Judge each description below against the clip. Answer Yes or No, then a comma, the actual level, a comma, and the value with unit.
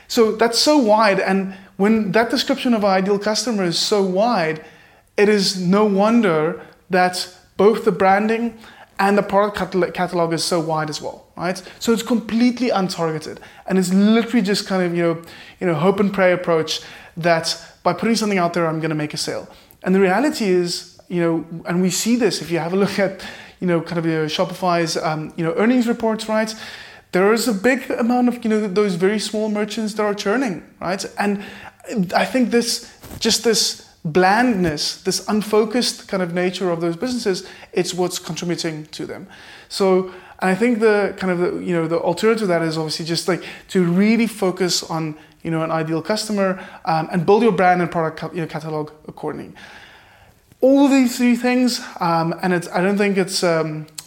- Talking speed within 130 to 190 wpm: No, average, 200 wpm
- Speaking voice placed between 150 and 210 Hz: Yes, high, 190 Hz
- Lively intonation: No, average, 4.2 semitones